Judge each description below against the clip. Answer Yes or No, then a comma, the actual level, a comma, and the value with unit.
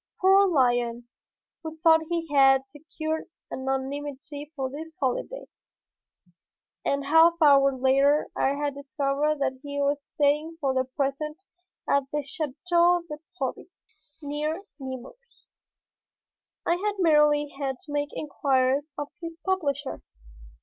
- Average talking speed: No, slow, 120 wpm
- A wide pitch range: No, average, 2.7 semitones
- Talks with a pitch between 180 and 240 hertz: No, very high, 290 Hz